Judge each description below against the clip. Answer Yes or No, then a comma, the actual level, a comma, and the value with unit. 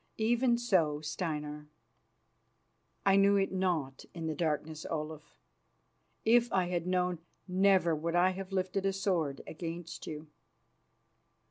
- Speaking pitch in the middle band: Yes, medium, 175 Hz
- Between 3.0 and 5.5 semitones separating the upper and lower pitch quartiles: Yes, average, 3.7 semitones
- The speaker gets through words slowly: Yes, slow, 120 wpm